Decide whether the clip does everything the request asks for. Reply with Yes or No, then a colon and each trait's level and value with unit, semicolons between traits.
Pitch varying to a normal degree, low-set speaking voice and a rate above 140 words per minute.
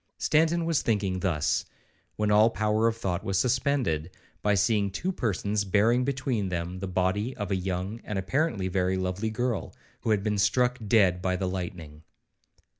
Yes: average, 3.8 semitones; low, 100 Hz; average, 170 wpm